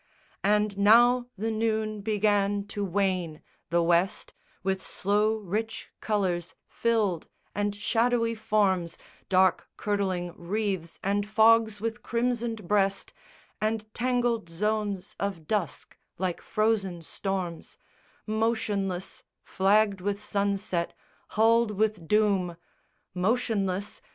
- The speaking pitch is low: No, high, 205 Hz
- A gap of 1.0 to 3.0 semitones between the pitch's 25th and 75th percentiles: Yes, narrow, 2.5 semitones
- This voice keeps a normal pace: No, slow, 100 wpm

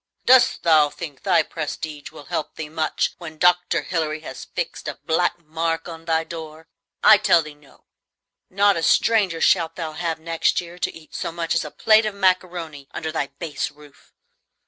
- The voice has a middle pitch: Yes, medium, 165 Hz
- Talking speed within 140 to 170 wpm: No, average, 185 wpm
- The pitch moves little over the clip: Yes, narrow, 2.2 semitones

